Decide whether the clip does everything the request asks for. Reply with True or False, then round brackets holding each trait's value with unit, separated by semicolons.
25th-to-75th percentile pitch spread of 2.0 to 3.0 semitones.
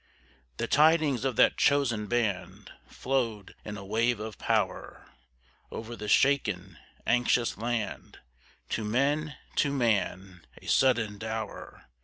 False (4.0 semitones)